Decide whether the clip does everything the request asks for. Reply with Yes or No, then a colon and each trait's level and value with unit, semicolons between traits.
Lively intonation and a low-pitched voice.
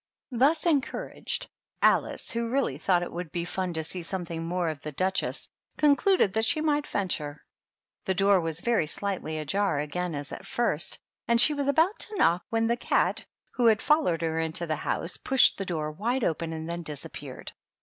No: wide, 6.7 semitones; medium, 185 Hz